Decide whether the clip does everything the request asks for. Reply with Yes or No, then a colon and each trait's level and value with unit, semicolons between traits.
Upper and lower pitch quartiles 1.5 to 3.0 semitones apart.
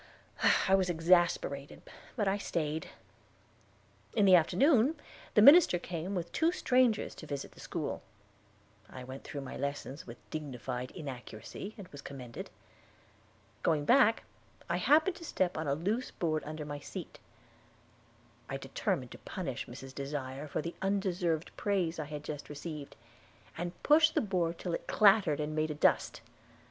No: wide, 5.4 semitones